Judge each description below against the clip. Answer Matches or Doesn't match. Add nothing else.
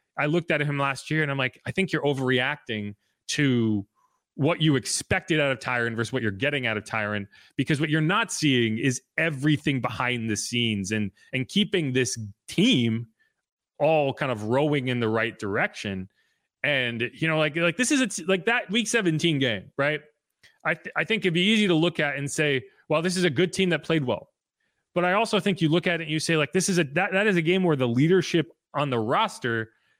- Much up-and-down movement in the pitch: Matches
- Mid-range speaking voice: Matches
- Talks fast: Matches